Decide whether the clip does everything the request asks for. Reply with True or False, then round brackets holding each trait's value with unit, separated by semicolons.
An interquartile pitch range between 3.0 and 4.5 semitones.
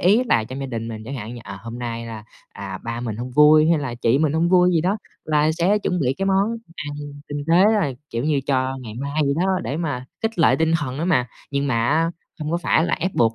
False (5.6 semitones)